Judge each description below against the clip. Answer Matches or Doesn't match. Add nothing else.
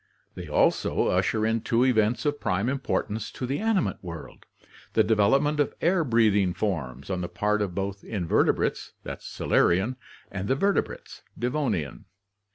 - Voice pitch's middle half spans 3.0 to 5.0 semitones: Doesn't match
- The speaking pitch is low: Matches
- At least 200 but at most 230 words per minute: Doesn't match